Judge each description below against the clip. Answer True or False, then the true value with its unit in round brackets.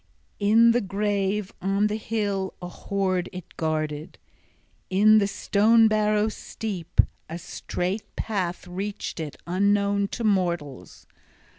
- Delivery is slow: True (120 wpm)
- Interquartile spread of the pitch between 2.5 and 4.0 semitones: True (2.9 semitones)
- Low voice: False (200 Hz)